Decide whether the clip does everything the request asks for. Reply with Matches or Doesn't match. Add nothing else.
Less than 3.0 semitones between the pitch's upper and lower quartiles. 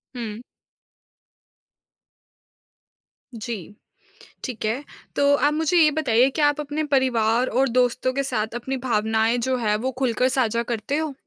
Doesn't match